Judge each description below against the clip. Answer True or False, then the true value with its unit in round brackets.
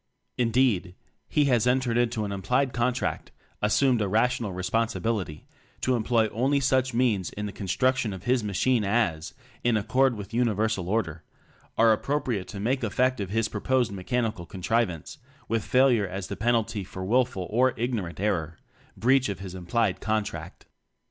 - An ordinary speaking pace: True (165 wpm)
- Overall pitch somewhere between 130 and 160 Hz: False (115 Hz)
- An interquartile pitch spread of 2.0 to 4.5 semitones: True (4.1 semitones)